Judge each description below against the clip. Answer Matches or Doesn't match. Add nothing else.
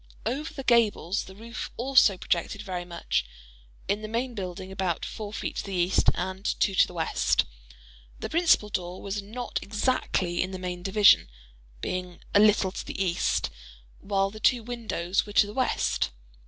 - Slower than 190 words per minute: Matches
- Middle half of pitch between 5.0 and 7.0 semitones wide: Doesn't match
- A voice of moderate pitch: Doesn't match